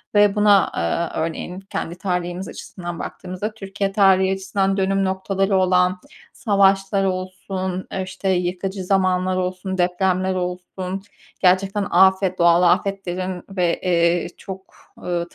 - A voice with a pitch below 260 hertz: Yes, medium, 185 Hz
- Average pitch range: No, narrow, 1.3 semitones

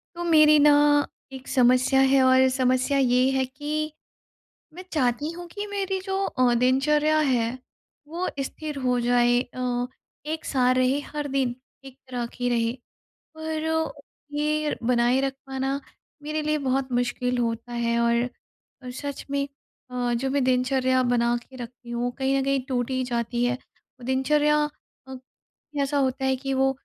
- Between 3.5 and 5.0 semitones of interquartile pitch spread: No, average, 3.1 semitones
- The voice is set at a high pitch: Yes, very high, 265 Hz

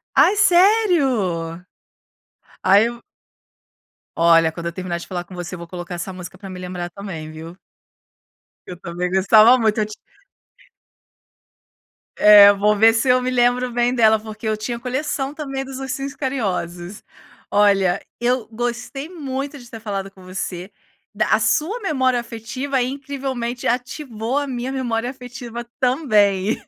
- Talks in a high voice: Yes, high, 225 Hz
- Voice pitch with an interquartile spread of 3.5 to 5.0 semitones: No, wide, 5.6 semitones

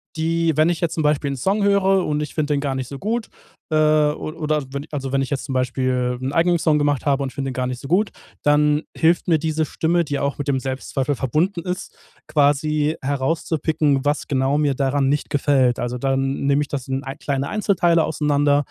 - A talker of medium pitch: Yes, medium, 145 Hz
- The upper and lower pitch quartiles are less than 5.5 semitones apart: Yes, average, 2.7 semitones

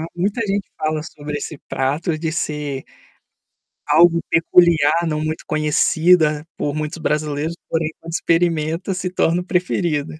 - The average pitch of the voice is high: No, medium, 160 Hz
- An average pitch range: No, narrow, 2.3 semitones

